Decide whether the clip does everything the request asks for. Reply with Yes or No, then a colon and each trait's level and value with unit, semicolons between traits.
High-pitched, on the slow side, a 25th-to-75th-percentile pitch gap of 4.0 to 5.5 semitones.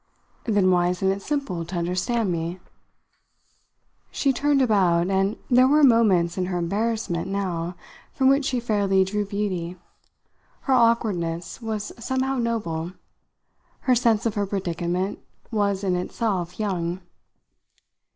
Yes: high, 195 Hz; slow, 130 wpm; average, 4.5 semitones